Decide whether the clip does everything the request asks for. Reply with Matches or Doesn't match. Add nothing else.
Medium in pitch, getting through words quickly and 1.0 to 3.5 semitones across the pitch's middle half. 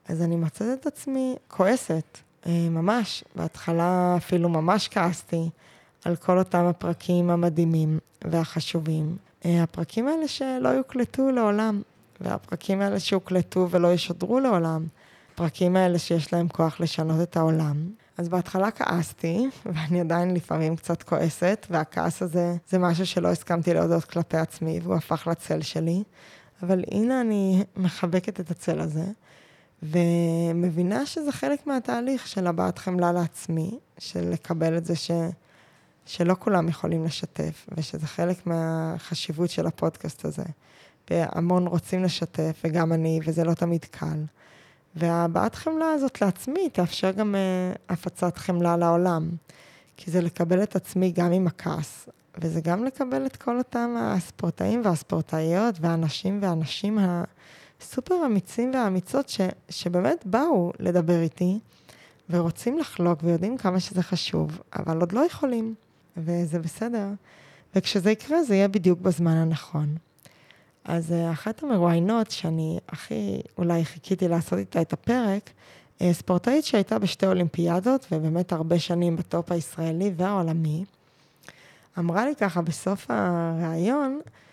Doesn't match